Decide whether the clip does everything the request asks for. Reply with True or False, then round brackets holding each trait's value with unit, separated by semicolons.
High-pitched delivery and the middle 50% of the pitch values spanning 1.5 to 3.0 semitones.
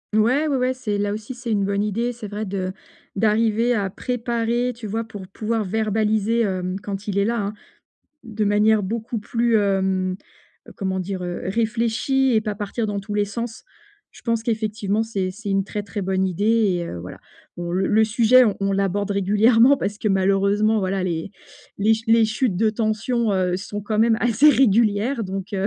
True (210 Hz; 2.6 semitones)